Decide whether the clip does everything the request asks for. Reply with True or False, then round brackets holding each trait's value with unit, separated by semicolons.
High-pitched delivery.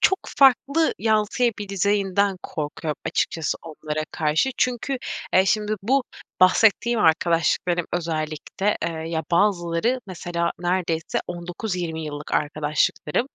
False (175 Hz)